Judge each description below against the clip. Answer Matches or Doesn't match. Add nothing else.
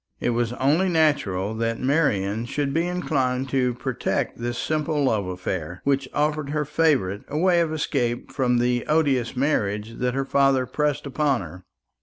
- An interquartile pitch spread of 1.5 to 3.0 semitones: Doesn't match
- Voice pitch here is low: Matches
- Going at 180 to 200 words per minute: Doesn't match